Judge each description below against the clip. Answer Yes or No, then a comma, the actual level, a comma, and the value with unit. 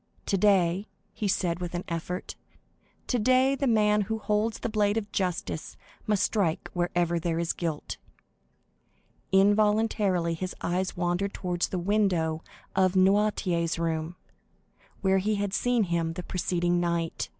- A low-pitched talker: No, medium, 185 Hz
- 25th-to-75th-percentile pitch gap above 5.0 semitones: No, average, 3.4 semitones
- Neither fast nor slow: No, slow, 130 wpm